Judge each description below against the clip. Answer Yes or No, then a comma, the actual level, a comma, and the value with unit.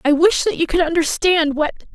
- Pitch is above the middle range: Yes, very high, 325 Hz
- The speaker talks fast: Yes, fast, 215 wpm